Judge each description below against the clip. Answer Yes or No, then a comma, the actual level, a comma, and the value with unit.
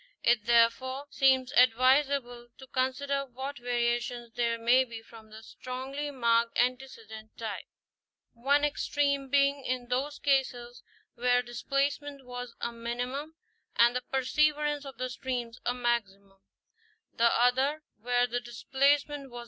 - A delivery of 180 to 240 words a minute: No, slow, 135 wpm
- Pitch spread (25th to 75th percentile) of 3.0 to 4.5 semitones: No, narrow, 2.6 semitones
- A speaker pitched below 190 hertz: No, very high, 250 Hz